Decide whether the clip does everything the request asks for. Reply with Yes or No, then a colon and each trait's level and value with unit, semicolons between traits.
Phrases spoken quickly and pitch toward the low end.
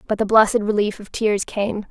No: fast, 220 wpm; high, 210 Hz